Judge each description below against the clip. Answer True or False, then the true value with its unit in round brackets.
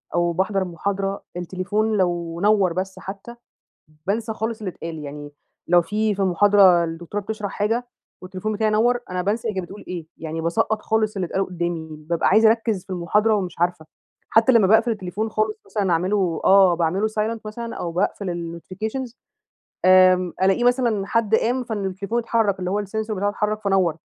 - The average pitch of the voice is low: False (195 Hz)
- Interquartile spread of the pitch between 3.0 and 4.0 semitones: True (3.5 semitones)